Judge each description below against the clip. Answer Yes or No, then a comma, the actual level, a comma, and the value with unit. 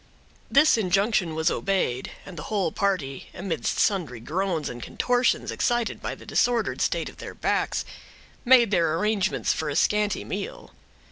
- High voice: Yes, high, 195 Hz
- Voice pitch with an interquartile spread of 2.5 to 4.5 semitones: No, wide, 5.5 semitones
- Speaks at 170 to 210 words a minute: No, average, 150 wpm